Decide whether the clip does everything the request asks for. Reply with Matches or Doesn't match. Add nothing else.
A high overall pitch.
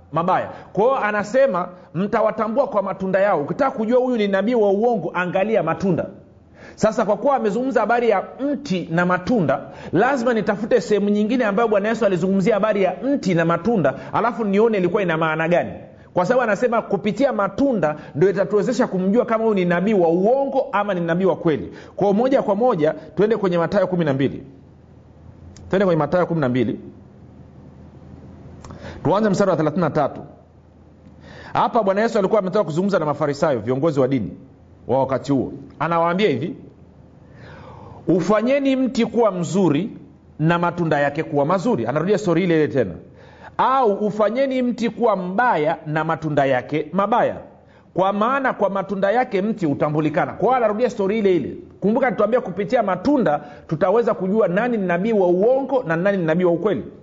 Matches